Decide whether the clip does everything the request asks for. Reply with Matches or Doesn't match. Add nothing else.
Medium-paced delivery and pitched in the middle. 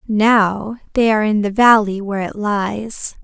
Doesn't match